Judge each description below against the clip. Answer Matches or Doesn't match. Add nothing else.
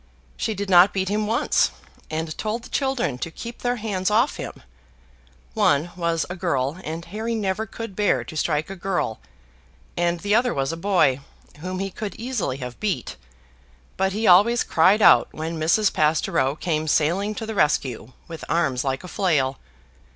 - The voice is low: Doesn't match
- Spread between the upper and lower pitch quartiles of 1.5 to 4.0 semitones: Doesn't match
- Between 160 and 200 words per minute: Matches